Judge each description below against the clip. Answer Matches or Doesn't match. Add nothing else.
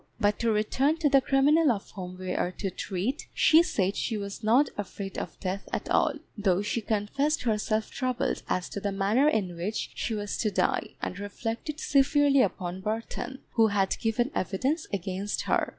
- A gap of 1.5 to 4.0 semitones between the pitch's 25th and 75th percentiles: Doesn't match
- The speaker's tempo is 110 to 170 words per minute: Doesn't match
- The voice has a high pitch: Matches